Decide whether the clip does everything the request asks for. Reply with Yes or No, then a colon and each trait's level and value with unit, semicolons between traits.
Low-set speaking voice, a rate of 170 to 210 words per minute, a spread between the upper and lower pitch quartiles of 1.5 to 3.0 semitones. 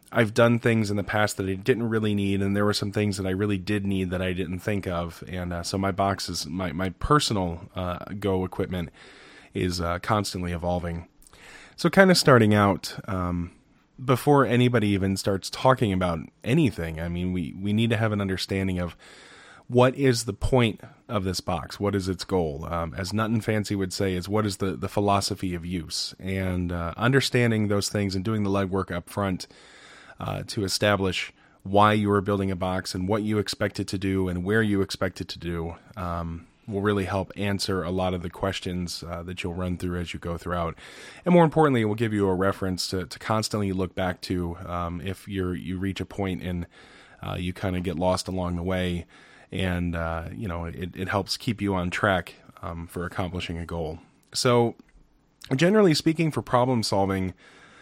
Yes: very low, 95 Hz; fast, 205 wpm; average, 2.7 semitones